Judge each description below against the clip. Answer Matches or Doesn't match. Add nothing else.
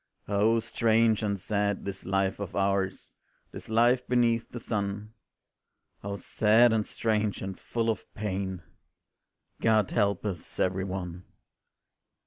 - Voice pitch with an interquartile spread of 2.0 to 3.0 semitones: Matches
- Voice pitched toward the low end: Matches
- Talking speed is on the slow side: Matches